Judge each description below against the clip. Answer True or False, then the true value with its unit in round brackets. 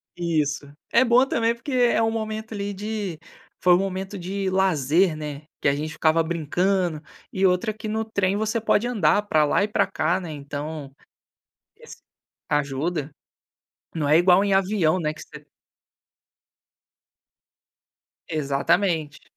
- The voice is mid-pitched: True (180 Hz)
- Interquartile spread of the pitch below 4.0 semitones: False (5.2 semitones)